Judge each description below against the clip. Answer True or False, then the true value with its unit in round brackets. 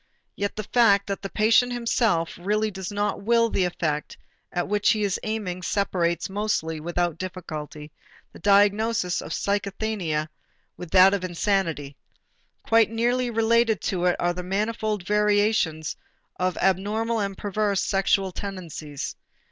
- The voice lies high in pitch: True (200 Hz)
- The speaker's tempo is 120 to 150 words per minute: True (140 wpm)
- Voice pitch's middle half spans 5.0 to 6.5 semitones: False (3.4 semitones)